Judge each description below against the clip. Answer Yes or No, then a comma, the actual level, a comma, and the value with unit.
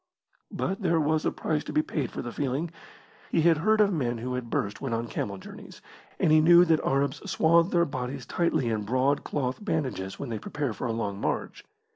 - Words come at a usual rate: No, fast, 220 wpm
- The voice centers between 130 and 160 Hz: Yes, medium, 140 Hz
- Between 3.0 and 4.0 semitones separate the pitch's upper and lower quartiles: No, average, 5.2 semitones